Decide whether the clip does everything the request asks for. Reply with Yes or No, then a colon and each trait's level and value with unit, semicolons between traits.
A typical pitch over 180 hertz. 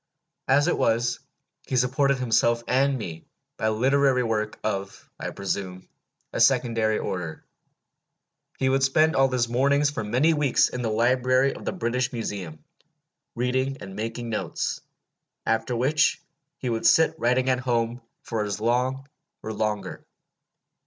No: low, 120 Hz